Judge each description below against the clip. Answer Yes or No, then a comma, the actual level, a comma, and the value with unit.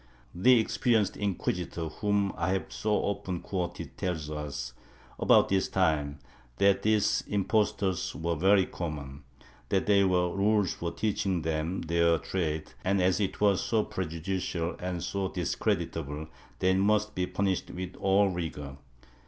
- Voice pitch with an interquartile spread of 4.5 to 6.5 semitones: No, average, 3.3 semitones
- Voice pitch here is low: Yes, very low, 95 Hz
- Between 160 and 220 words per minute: No, average, 145 wpm